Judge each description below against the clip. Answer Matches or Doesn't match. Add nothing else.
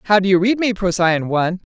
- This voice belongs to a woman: Matches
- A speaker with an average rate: Doesn't match